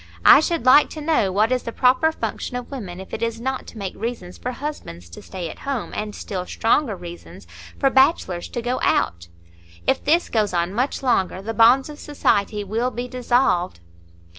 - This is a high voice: Yes, high, 230 Hz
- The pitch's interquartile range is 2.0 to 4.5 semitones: No, wide, 5.6 semitones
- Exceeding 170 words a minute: Yes, average, 195 wpm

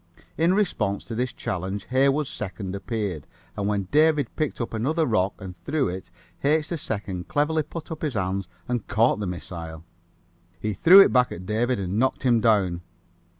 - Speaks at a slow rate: No, average, 175 wpm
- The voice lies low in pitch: Yes, low, 110 Hz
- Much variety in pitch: Yes, wide, 6.9 semitones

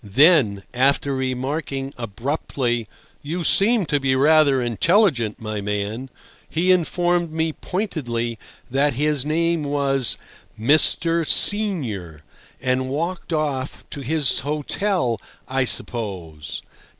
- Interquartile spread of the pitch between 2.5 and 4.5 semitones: No, average, 5.2 semitones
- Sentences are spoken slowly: Yes, slow, 100 wpm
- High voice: No, medium, 140 Hz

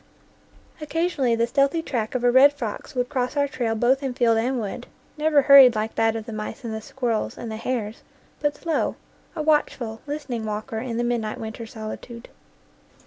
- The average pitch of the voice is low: No, high, 245 Hz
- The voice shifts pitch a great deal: No, average, 3.7 semitones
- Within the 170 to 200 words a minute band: Yes, average, 190 wpm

